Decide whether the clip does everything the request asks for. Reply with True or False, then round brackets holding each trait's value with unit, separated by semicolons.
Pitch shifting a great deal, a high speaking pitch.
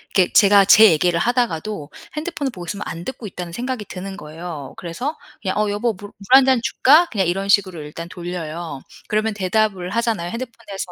False (4.9 semitones; 200 Hz)